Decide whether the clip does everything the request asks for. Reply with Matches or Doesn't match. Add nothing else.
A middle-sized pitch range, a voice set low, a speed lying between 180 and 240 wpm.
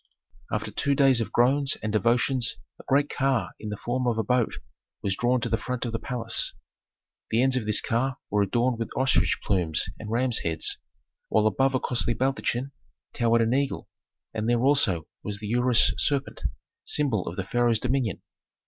Matches